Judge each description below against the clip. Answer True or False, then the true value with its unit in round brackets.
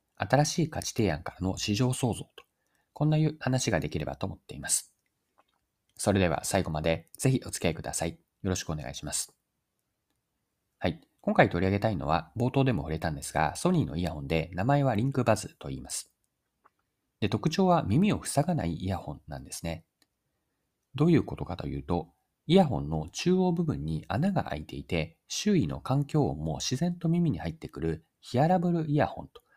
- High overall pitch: False (105 Hz)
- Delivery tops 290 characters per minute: True (365 characters per minute)